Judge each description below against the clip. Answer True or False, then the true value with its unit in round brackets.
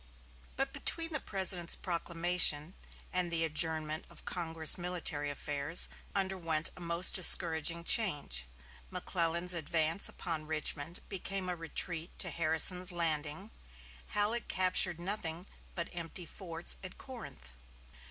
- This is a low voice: False (170 Hz)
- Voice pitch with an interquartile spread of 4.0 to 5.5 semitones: False (2.5 semitones)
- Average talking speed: False (115 wpm)